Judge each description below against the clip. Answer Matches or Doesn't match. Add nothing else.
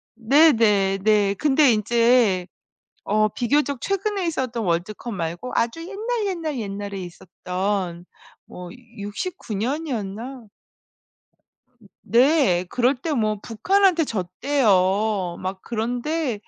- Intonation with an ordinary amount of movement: Doesn't match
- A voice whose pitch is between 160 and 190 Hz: Doesn't match